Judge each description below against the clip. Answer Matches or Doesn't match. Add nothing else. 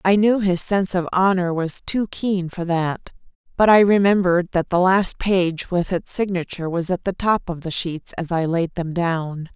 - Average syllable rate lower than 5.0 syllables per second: Matches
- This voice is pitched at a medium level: Matches